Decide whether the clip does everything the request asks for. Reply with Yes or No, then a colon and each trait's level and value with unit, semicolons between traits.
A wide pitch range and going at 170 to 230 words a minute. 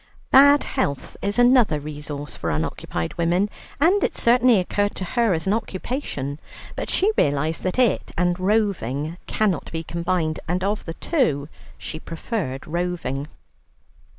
No: wide, 6.4 semitones; average, 145 wpm